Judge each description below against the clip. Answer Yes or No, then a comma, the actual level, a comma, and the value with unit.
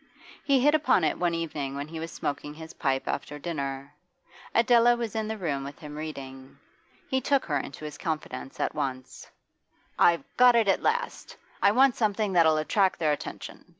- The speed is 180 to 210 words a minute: Yes, average, 185 wpm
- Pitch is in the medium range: Yes, medium, 165 Hz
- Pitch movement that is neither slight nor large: No, wide, 7.5 semitones